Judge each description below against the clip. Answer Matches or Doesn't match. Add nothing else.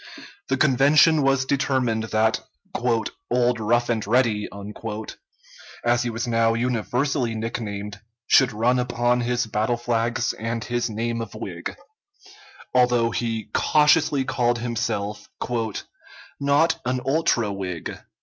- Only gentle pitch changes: Matches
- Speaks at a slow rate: Matches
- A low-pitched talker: Matches